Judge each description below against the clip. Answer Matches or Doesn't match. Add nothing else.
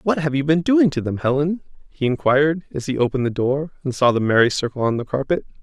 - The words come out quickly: Matches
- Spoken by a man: Matches